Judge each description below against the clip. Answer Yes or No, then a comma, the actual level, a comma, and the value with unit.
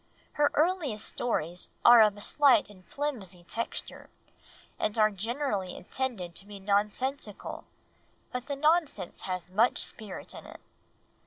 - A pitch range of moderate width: No, wide, 5.7 semitones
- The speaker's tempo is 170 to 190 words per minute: No, slow, 135 wpm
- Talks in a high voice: Yes, high, 215 Hz